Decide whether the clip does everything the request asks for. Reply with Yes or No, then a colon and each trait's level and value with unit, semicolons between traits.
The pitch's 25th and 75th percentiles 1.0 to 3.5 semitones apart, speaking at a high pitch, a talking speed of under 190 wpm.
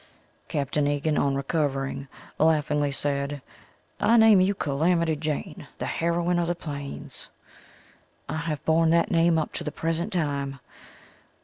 No: average, 2.9 semitones; medium, 155 Hz; slow, 135 wpm